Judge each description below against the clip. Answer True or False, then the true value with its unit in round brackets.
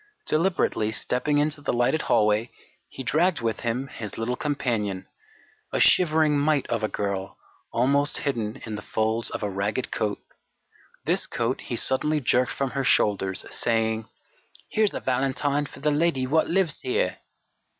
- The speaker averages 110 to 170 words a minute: True (155 wpm)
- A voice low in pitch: True (130 Hz)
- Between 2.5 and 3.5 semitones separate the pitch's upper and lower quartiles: False (5.1 semitones)